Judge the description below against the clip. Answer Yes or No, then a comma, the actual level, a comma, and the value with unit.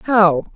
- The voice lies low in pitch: No, high, 190 Hz